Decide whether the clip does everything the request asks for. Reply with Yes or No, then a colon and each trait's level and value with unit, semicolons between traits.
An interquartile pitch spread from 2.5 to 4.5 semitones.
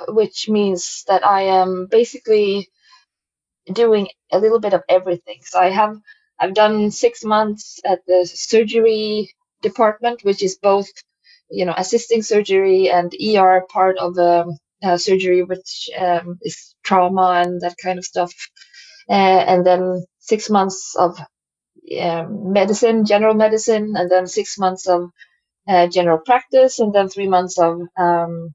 Yes: average, 3.3 semitones